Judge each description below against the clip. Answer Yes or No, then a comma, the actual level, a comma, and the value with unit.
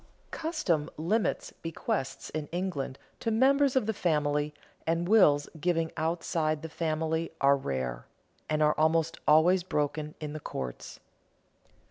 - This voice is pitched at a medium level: Yes, medium, 160 Hz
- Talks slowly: Yes, slow, 130 wpm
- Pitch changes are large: No, average, 3.0 semitones